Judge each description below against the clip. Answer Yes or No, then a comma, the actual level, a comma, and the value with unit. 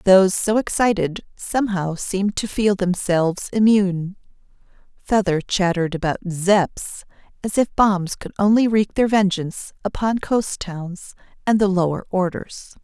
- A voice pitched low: No, high, 195 Hz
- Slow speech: Yes, slow, 130 wpm